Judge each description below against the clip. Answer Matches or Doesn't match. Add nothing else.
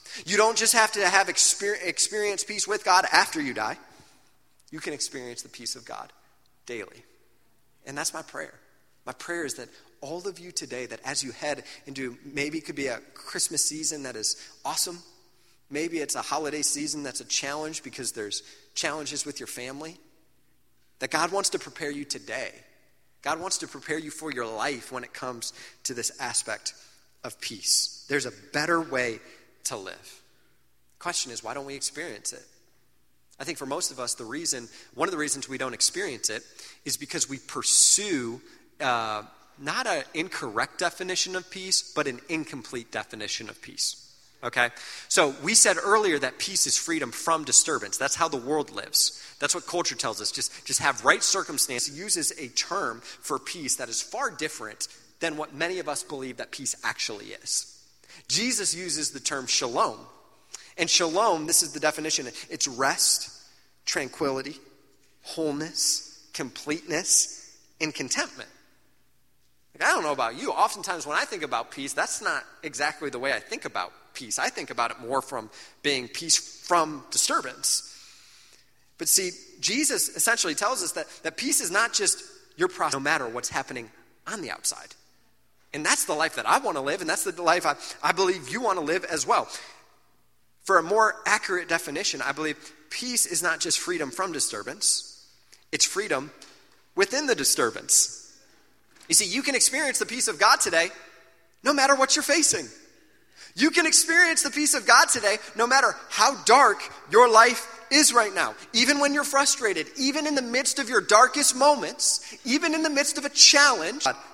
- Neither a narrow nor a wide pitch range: Doesn't match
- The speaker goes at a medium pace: Matches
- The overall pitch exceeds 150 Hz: Matches